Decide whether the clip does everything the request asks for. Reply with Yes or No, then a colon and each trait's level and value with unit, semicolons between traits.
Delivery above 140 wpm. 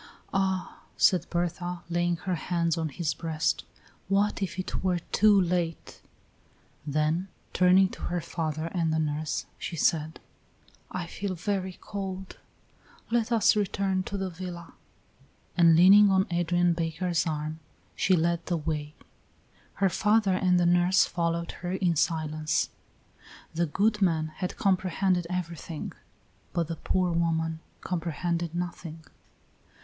No: slow, 135 wpm